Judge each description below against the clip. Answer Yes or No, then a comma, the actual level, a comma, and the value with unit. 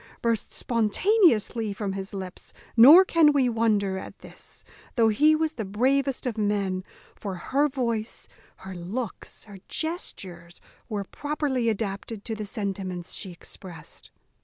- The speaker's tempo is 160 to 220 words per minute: No, slow, 135 wpm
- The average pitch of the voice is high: Yes, high, 220 Hz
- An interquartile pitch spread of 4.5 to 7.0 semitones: Yes, average, 5.2 semitones